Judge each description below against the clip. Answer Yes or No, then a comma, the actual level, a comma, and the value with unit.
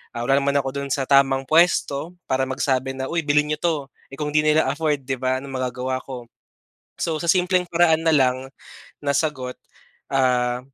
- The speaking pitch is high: No, medium, 140 Hz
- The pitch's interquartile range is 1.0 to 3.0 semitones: Yes, average, 2.7 semitones